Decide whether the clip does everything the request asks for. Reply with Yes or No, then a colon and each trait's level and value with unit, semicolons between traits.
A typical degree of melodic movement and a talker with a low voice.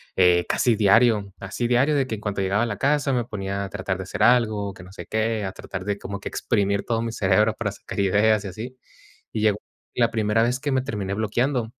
Yes: average, 3.1 semitones; low, 110 Hz